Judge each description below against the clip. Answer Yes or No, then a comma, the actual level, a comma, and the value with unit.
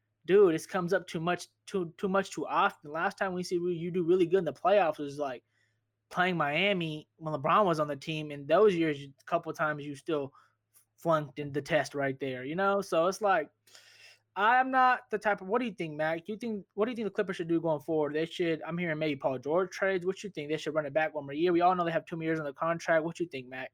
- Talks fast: Yes, fast, 275 wpm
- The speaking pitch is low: No, medium, 165 Hz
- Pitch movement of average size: Yes, average, 4.3 semitones